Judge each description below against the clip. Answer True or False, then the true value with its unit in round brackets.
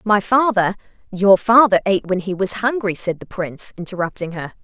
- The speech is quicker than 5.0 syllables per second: True (5.5 syllables/s)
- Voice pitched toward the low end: False (200 Hz)